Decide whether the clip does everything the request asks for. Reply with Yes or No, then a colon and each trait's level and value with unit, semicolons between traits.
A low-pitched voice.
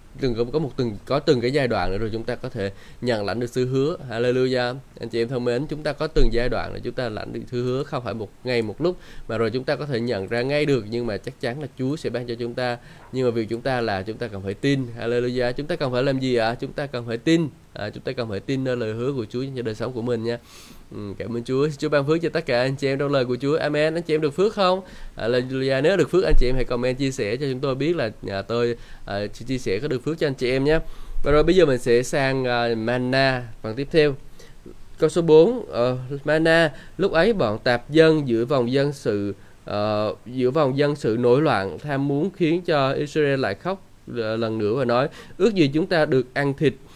Yes: low, 125 Hz